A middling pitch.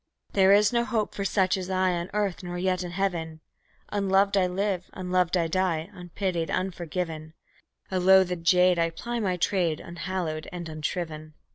Yes: medium, 180 Hz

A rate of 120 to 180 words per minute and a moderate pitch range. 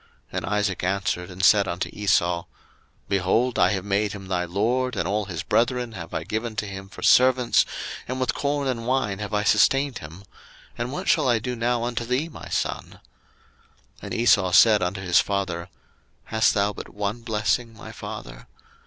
No: average, 190 wpm; average, 4.1 semitones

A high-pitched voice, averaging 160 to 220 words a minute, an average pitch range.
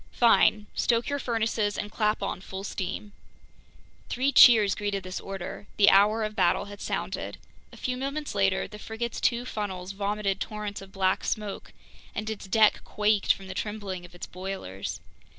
No: high, 205 Hz; average, 170 wpm; narrow, 2.1 semitones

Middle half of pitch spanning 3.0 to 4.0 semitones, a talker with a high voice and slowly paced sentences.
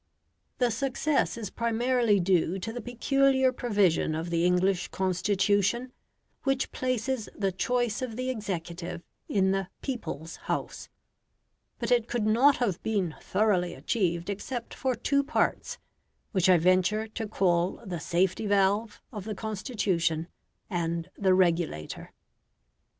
No: average, 5.0 semitones; high, 205 Hz; slow, 130 wpm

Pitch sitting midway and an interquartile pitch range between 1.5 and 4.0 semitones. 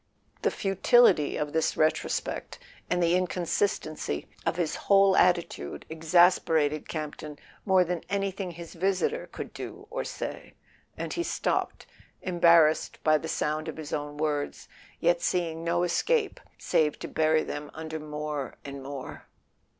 Yes: medium, 160 Hz; average, 2.8 semitones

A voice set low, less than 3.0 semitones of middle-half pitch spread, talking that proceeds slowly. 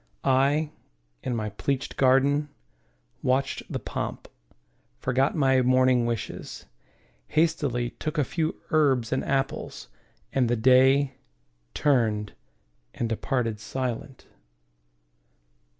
Yes: low, 130 Hz; narrow, 2.4 semitones; slow, 100 wpm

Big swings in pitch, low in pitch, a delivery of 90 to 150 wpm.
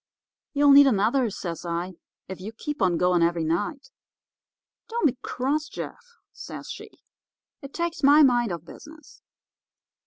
No: wide, 8.4 semitones; high, 240 Hz; average, 145 wpm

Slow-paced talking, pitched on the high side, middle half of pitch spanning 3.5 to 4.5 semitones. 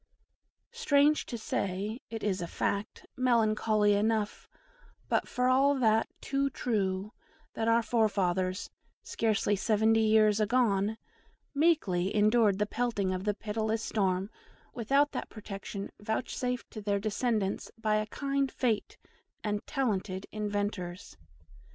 No: slow, 120 wpm; high, 215 Hz; average, 2.9 semitones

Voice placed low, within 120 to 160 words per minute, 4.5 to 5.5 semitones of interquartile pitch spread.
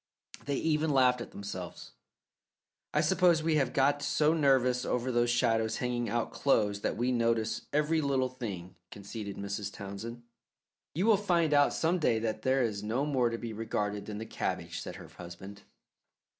No: low, 120 Hz; average, 170 wpm; average, 5.0 semitones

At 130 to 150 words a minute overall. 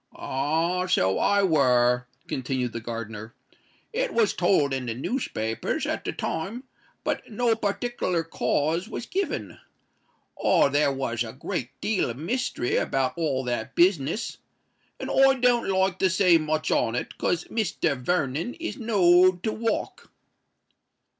Yes: average, 140 wpm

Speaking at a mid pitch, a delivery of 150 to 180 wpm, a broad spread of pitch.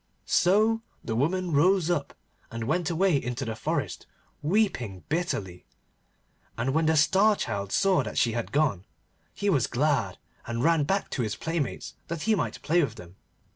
Yes: medium, 150 Hz; average, 170 wpm; wide, 7.3 semitones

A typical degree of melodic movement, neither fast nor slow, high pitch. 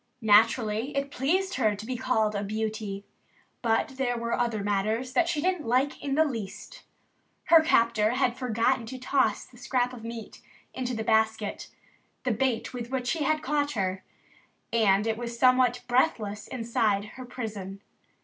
Yes: average, 3.1 semitones; average, 165 wpm; high, 235 Hz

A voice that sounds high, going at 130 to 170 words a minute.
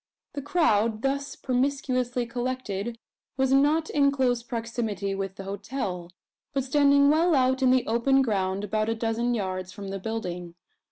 Yes: high, 240 Hz; average, 155 wpm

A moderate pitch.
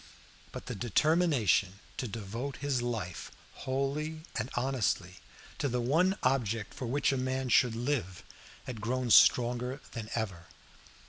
No: low, 125 Hz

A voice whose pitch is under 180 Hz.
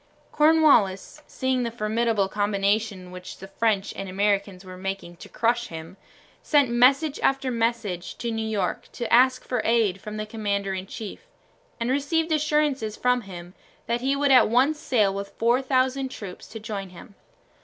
No: high, 225 Hz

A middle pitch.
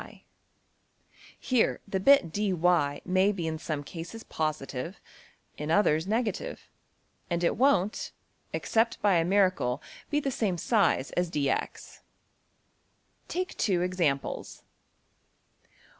Yes: medium, 180 Hz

